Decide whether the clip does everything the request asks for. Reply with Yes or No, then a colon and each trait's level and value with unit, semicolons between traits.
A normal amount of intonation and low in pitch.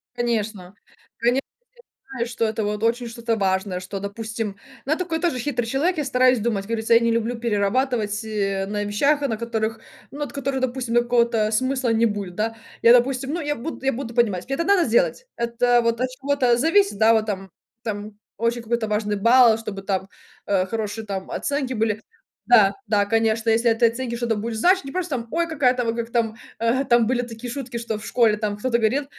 No: average, 3.0 semitones; high, 230 Hz